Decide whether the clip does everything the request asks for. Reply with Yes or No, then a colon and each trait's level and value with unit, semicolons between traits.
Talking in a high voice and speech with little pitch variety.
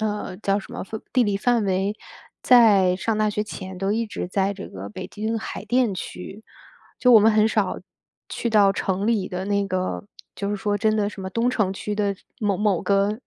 Yes: high, 205 Hz; narrow, 2.0 semitones